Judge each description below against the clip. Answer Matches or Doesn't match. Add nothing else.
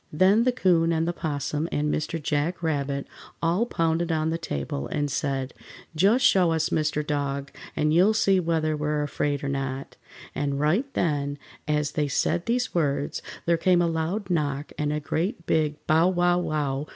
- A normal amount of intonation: Matches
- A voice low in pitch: Doesn't match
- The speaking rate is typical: Matches